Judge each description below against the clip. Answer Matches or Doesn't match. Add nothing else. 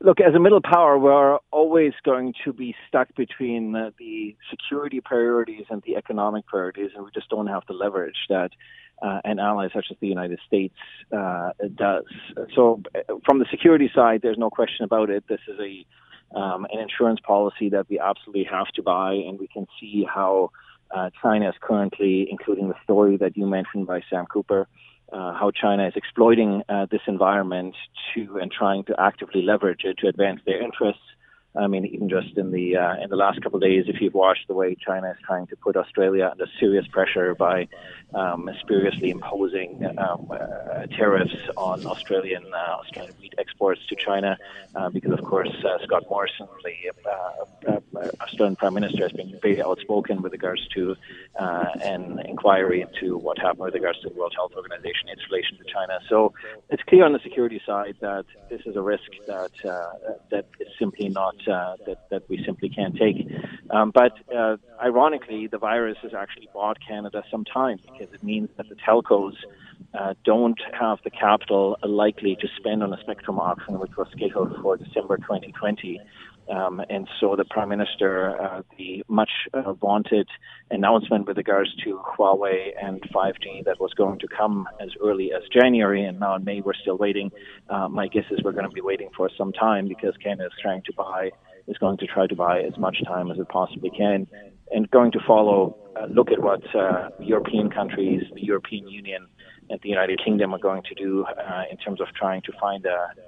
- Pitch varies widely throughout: Doesn't match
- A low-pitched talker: Matches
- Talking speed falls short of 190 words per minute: Doesn't match